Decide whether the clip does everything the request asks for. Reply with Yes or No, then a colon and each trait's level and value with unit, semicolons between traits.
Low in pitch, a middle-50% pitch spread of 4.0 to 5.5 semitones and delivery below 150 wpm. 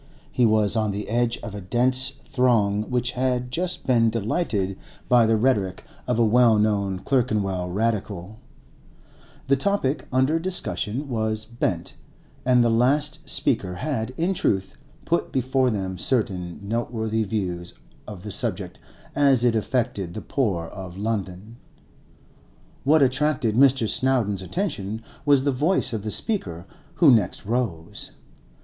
Yes: low, 115 Hz; average, 4.4 semitones; average, 140 wpm